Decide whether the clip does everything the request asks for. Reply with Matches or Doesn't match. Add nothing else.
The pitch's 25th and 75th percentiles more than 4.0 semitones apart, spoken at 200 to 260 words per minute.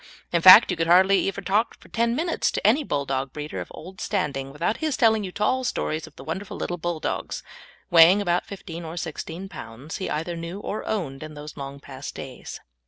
Matches